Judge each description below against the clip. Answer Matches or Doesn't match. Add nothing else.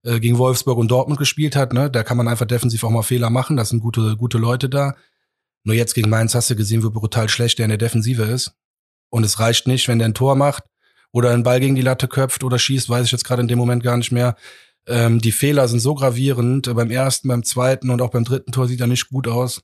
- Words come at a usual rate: Doesn't match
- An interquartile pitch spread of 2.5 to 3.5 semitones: Doesn't match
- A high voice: Doesn't match